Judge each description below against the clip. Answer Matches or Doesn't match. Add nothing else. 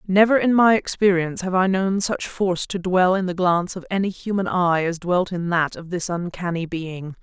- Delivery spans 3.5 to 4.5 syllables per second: Doesn't match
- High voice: Doesn't match